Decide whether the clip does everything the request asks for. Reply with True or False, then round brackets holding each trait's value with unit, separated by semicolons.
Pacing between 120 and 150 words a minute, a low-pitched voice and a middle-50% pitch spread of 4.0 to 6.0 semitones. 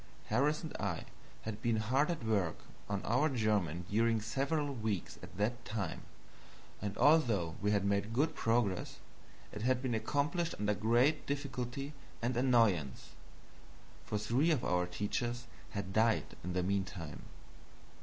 True (145 wpm; 115 Hz; 4.5 semitones)